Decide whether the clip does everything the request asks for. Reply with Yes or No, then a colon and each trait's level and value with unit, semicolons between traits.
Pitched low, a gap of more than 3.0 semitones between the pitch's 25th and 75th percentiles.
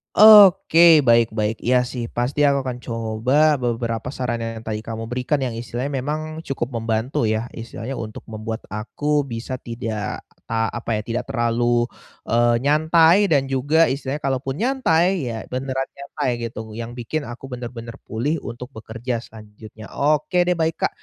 Yes: low, 125 Hz; average, 4.0 semitones